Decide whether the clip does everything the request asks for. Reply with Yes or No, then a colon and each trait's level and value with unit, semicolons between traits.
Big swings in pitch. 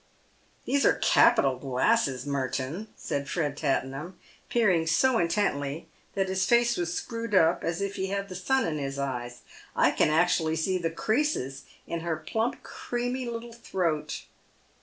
Yes: wide, 7.4 semitones